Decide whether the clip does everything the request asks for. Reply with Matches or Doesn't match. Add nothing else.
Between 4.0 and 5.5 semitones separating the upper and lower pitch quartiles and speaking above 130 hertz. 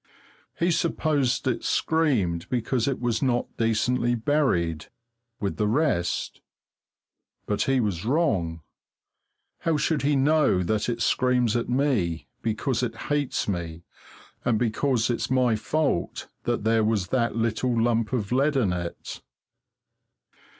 Doesn't match